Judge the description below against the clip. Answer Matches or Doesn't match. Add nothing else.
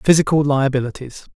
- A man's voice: Matches